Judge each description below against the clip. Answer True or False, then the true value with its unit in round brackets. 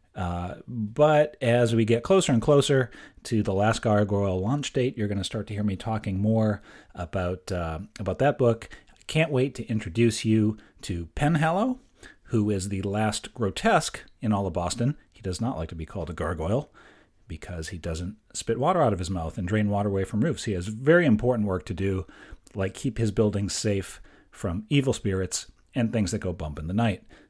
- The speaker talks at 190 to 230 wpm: True (200 wpm)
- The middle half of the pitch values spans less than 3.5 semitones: False (4.0 semitones)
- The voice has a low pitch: True (105 Hz)